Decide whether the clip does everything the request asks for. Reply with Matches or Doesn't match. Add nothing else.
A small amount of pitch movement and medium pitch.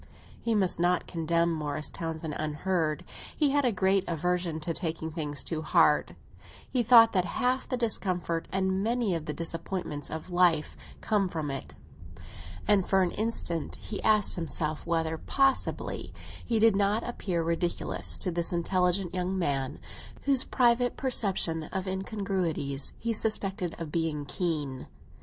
Doesn't match